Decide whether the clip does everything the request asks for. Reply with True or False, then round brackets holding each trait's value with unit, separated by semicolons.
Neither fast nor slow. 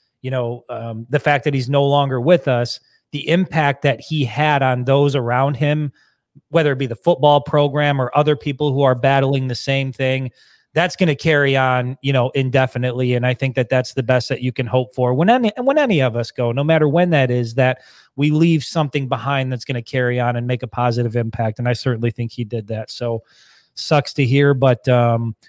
False (225 wpm)